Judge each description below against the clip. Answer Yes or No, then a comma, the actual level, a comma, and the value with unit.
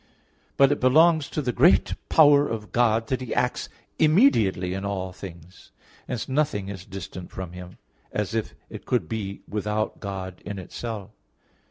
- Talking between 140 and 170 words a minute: Yes, average, 160 wpm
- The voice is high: No, low, 105 Hz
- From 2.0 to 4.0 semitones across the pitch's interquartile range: No, average, 5.3 semitones